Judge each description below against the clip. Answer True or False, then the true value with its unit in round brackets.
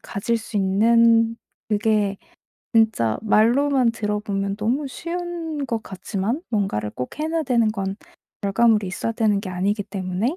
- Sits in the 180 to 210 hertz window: False (220 Hz)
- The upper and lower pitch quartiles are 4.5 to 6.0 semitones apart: False (3.1 semitones)